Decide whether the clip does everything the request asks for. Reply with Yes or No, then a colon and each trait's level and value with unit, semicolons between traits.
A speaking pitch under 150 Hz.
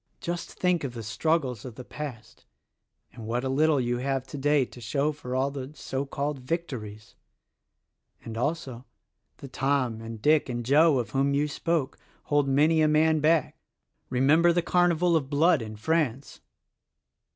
Yes: medium, 140 Hz